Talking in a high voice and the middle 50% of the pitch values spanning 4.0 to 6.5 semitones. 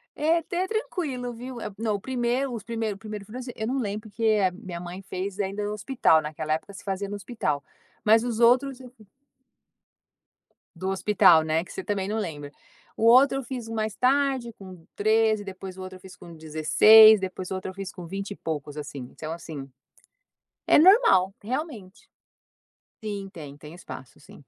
Yes: high, 205 Hz; average, 4.5 semitones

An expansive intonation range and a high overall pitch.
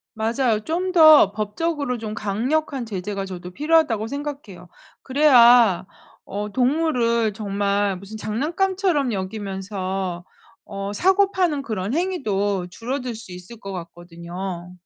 Yes: wide, 6.5 semitones; high, 220 Hz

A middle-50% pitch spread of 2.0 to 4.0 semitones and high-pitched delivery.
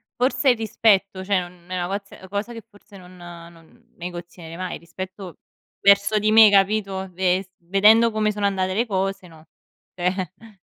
Yes: average, 2.7 semitones; high, 195 Hz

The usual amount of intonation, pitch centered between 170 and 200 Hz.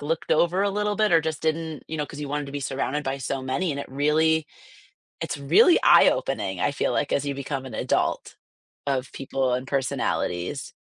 No: average, 3.0 semitones; medium, 145 Hz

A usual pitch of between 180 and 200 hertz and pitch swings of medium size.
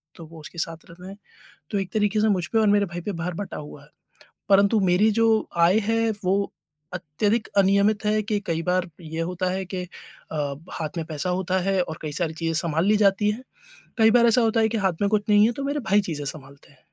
Yes: high, 190 Hz; average, 4.2 semitones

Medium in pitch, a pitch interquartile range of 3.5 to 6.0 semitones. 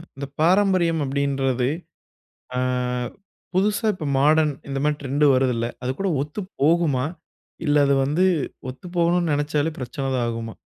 Yes: medium, 145 Hz; average, 4.1 semitones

